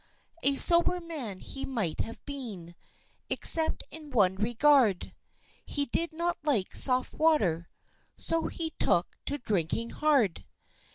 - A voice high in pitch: Yes, very high, 270 Hz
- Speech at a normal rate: No, slow, 125 wpm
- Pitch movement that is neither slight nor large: No, wide, 7.2 semitones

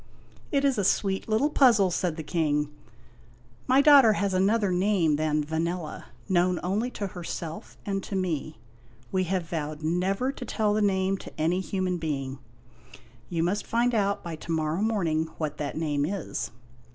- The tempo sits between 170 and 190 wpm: Yes, average, 175 wpm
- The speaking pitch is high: No, medium, 180 Hz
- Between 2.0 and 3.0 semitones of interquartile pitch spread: No, average, 4.4 semitones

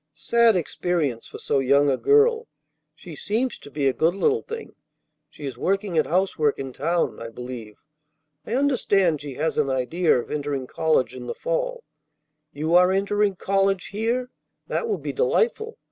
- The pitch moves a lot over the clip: Yes, wide, 8.7 semitones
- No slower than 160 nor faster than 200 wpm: Yes, average, 170 wpm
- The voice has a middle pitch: Yes, medium, 175 Hz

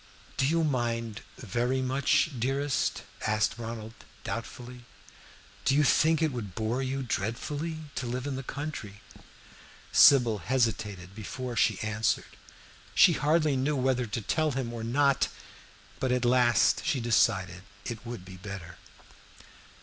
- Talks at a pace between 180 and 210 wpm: No, slow, 135 wpm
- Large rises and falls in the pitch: No, average, 3.7 semitones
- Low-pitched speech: Yes, low, 120 Hz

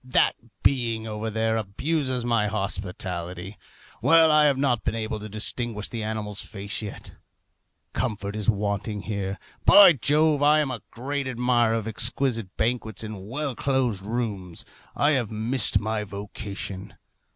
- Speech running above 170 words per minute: No, average, 145 wpm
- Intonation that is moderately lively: Yes, average, 3.8 semitones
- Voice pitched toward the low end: Yes, low, 110 Hz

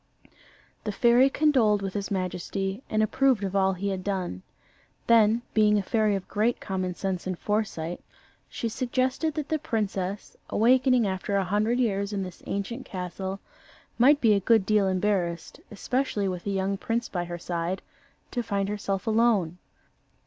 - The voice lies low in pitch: No, high, 200 Hz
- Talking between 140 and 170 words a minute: Yes, average, 165 wpm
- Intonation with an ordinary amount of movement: Yes, average, 3.4 semitones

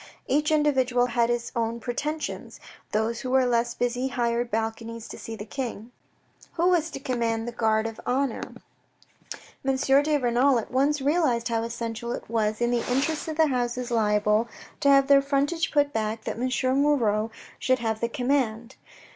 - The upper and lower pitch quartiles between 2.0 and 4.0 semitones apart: Yes, average, 3.3 semitones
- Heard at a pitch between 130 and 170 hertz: No, high, 245 Hz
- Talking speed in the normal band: Yes, average, 170 wpm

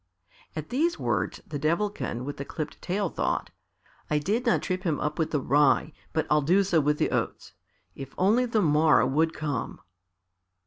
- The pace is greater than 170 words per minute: Yes, average, 180 wpm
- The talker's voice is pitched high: No, medium, 155 Hz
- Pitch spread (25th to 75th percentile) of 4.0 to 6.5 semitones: Yes, average, 4.6 semitones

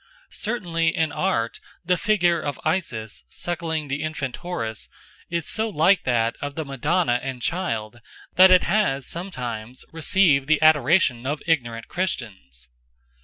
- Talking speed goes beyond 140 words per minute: No, slow, 135 wpm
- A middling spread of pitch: No, wide, 6.1 semitones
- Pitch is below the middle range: No, medium, 155 Hz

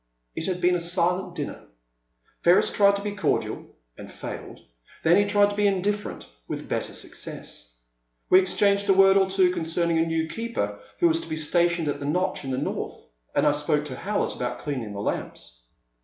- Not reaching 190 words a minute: No, average, 200 wpm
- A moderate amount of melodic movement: Yes, average, 4.2 semitones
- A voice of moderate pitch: Yes, medium, 180 Hz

